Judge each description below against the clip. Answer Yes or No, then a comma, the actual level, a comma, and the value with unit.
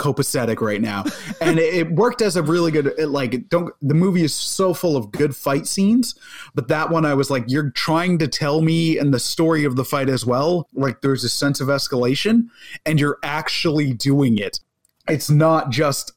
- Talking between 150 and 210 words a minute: Yes, fast, 205 wpm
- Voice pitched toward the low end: No, medium, 150 Hz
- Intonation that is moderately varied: Yes, average, 3.2 semitones